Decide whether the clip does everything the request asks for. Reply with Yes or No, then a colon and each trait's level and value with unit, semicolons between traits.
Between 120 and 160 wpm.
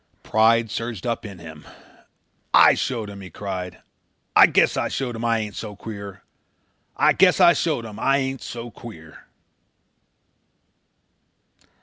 Yes: average, 140 wpm